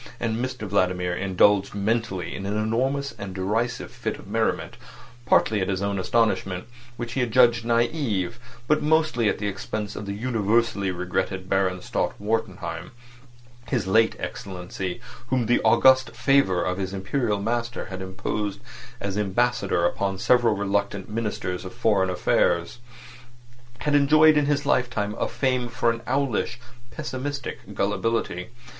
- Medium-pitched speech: No, low, 110 Hz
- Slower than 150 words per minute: Yes, average, 140 wpm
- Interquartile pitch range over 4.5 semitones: No, average, 4.0 semitones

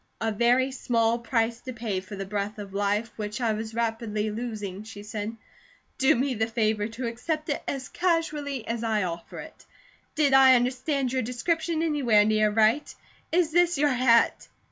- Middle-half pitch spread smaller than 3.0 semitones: No, average, 3.7 semitones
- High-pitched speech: Yes, high, 230 Hz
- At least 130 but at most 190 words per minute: Yes, average, 175 wpm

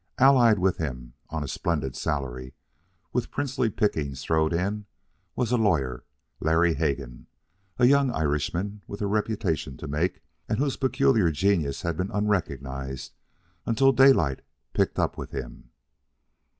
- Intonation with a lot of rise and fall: Yes, wide, 7.5 semitones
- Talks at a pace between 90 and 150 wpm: Yes, slow, 135 wpm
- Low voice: Yes, very low, 85 Hz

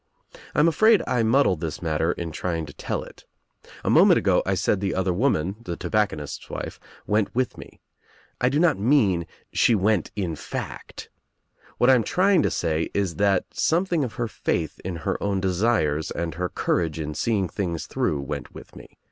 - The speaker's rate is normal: Yes, average, 190 wpm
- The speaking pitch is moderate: No, very low, 95 Hz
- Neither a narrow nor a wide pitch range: No, wide, 6.3 semitones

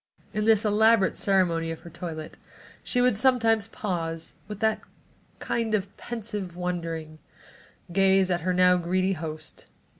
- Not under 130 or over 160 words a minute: Yes, average, 145 wpm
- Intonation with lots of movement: No, average, 4.1 semitones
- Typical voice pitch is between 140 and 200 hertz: Yes, high, 190 Hz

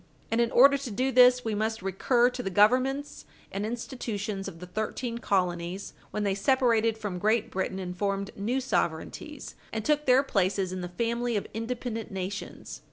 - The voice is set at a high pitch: Yes, high, 220 Hz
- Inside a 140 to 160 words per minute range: No, average, 175 wpm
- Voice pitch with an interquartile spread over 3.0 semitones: Yes, average, 4.2 semitones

